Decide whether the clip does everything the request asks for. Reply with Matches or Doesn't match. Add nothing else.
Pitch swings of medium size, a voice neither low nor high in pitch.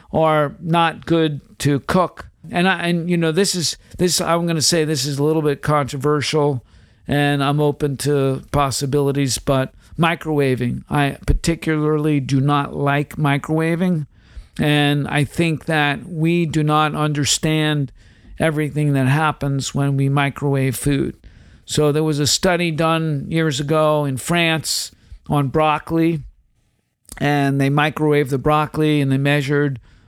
Doesn't match